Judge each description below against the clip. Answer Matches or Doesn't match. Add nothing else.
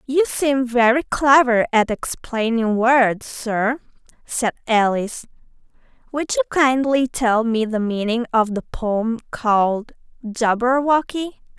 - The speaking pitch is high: Matches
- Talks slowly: Matches